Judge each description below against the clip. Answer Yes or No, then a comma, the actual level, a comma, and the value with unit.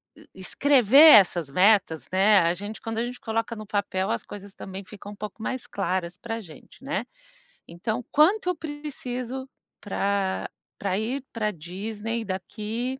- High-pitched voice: Yes, high, 215 Hz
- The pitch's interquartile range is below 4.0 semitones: No, average, 4.3 semitones